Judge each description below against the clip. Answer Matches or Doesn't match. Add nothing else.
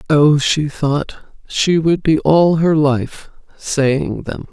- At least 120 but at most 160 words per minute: Matches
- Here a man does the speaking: Doesn't match